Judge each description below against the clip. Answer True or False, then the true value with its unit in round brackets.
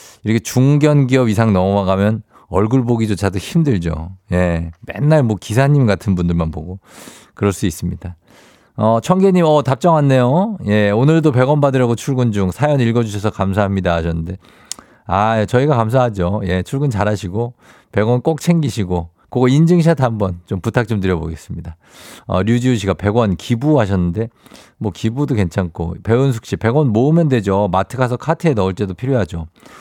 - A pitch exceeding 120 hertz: False (110 Hz)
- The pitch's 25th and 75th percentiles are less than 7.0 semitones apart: True (5.6 semitones)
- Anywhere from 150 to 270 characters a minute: False (335 characters per minute)